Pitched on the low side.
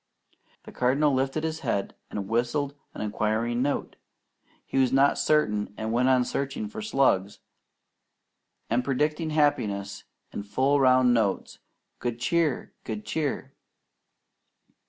Yes: low, 130 Hz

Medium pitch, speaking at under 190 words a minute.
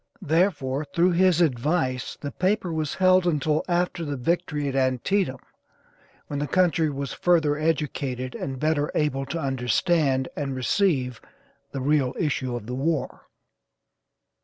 Yes: medium, 150 Hz; slow, 135 wpm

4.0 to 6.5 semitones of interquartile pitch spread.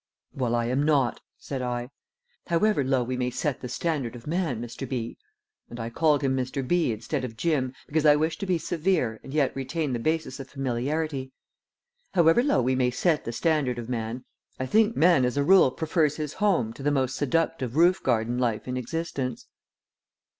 Yes: average, 4.3 semitones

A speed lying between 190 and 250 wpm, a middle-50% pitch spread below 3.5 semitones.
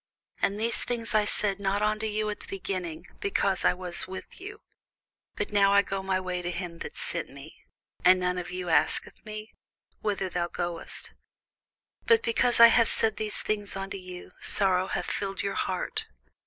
No: average, 180 wpm; average, 2.7 semitones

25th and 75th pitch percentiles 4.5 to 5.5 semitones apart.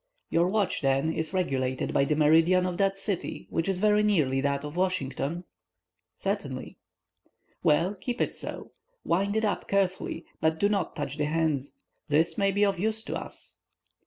Yes: average, 4.9 semitones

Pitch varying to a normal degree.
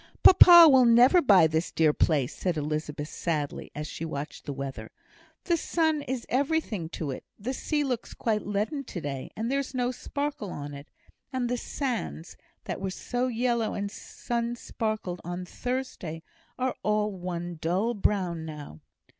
No: wide, 7.7 semitones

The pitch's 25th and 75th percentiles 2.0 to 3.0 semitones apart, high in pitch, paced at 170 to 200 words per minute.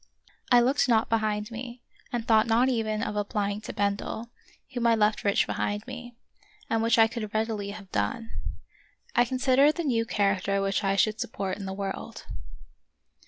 Yes: narrow, 2.6 semitones; high, 220 Hz; average, 175 wpm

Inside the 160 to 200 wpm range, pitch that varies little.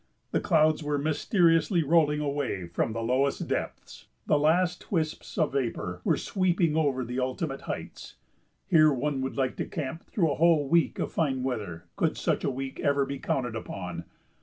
No: average, 175 wpm; average, 3.7 semitones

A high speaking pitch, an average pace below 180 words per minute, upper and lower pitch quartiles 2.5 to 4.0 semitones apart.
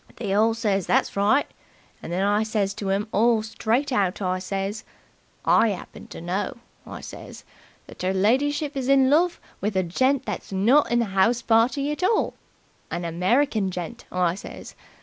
No: high, 215 Hz; average, 170 wpm; average, 4.7 semitones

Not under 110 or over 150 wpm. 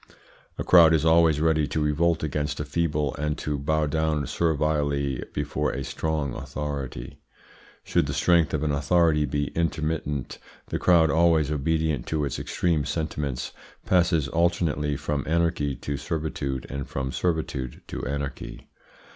Yes: average, 145 wpm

